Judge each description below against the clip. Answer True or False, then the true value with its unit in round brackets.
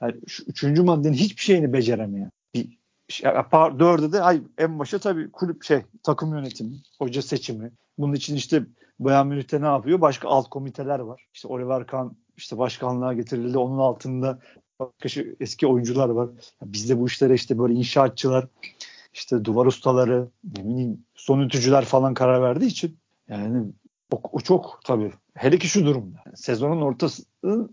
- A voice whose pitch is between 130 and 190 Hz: True (135 Hz)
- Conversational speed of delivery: False (160 wpm)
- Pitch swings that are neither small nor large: True (3.4 semitones)